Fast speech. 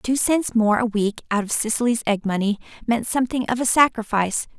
No: average, 195 wpm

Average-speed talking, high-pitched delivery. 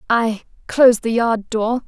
Yes: average, 160 wpm; high, 230 Hz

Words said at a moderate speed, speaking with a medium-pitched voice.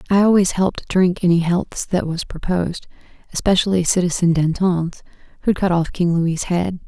Yes: average, 150 wpm; medium, 175 Hz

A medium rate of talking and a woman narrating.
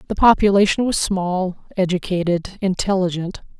No: slow, 100 wpm; female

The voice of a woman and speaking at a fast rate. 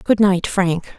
No: female; average, 185 wpm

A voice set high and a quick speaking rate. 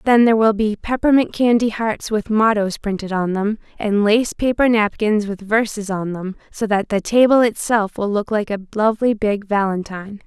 No: high, 215 Hz; average, 185 wpm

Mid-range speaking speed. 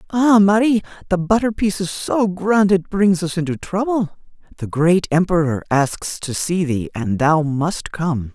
Yes: average, 175 wpm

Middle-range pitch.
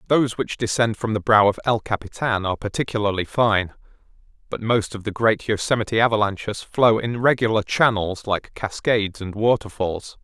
No: low, 110 Hz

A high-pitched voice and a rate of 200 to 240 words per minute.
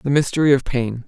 No: low, 135 Hz; fast, 225 wpm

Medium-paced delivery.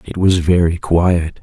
Yes: average, 170 wpm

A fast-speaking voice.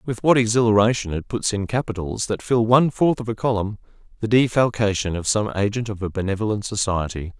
No: average, 185 wpm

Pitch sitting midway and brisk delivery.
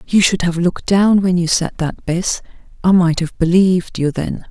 Yes: medium, 175 Hz; fast, 215 wpm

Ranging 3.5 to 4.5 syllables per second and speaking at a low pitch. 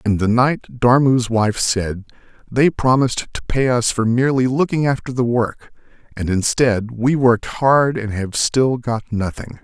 Yes: 4.4 syllables/s; low, 120 Hz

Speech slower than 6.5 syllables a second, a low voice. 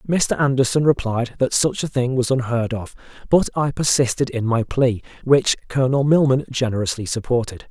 Yes: 5.2 syllables/s; low, 130 Hz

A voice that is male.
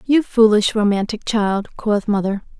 No: female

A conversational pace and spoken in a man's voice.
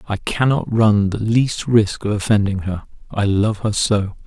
Yes: average, 170 wpm; male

